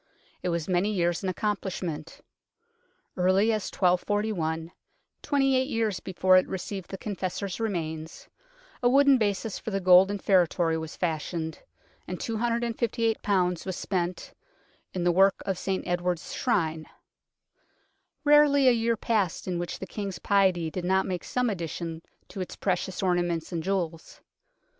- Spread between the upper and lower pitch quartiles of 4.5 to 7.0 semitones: No, average, 3.5 semitones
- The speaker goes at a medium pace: Yes, average, 145 wpm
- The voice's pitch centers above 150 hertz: Yes, medium, 185 Hz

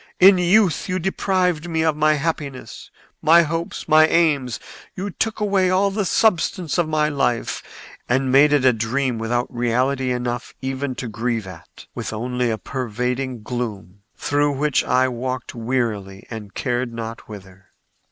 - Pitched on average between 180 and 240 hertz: No, low, 130 Hz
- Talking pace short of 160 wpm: Yes, average, 150 wpm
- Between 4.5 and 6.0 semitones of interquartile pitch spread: Yes, average, 5.1 semitones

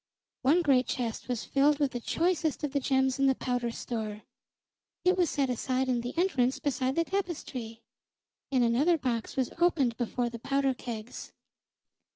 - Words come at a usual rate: Yes, average, 170 wpm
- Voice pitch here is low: No, very high, 265 Hz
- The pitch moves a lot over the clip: No, average, 3.4 semitones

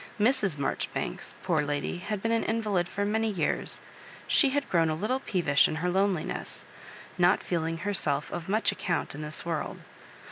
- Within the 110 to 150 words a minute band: No, average, 175 wpm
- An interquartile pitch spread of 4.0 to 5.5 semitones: Yes, average, 4.7 semitones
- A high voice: No, medium, 180 Hz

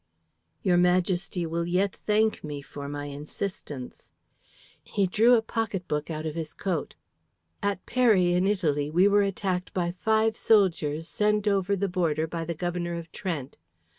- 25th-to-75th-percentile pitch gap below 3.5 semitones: No, average, 3.9 semitones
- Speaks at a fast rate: No, average, 160 wpm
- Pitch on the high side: No, medium, 180 Hz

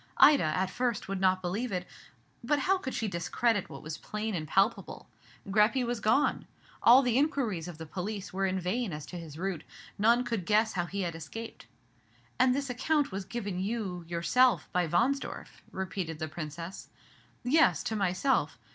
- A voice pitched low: No, high, 195 Hz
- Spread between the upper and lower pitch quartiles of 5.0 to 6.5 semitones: Yes, average, 5.3 semitones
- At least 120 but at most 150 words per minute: No, average, 180 wpm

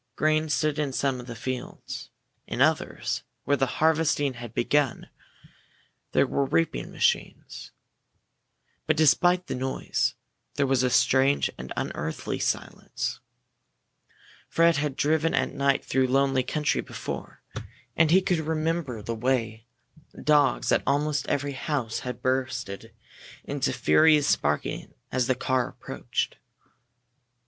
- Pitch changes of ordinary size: Yes, average, 3.3 semitones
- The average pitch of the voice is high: No, medium, 140 Hz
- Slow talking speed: Yes, slow, 125 wpm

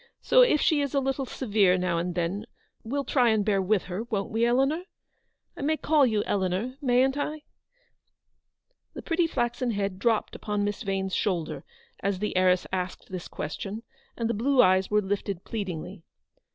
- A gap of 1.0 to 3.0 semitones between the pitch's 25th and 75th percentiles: No, wide, 5.6 semitones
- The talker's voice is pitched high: Yes, high, 210 Hz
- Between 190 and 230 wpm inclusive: No, average, 180 wpm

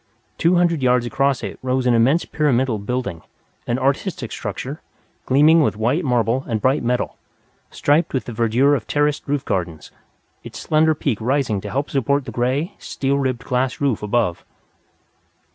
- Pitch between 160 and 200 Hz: No, low, 130 Hz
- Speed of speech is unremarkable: Yes, average, 160 wpm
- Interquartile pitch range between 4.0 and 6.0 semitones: No, average, 3.4 semitones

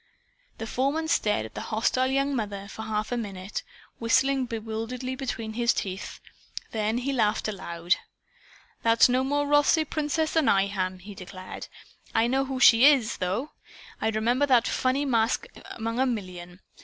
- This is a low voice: No, high, 230 Hz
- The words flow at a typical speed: Yes, average, 160 wpm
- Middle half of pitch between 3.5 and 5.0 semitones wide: Yes, average, 4.2 semitones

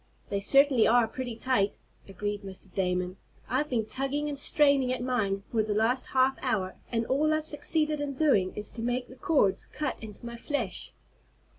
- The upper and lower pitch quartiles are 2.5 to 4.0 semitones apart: No, average, 5.1 semitones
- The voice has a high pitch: Yes, high, 245 Hz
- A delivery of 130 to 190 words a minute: Yes, average, 180 wpm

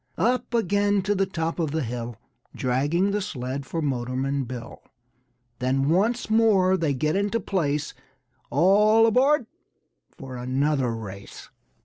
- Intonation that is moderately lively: No, wide, 7.8 semitones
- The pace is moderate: No, slow, 130 wpm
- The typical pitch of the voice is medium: Yes, medium, 160 Hz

